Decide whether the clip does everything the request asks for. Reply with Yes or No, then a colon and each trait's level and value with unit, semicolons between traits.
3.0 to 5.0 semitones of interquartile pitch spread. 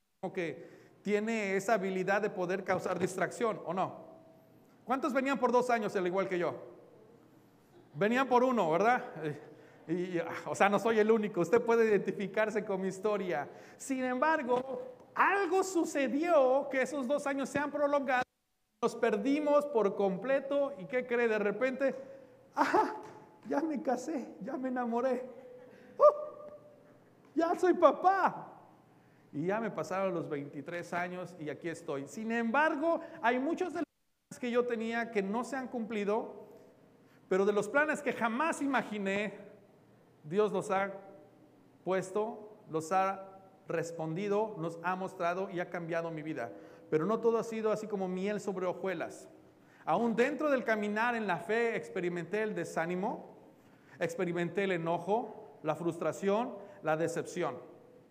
No: wide, 5.4 semitones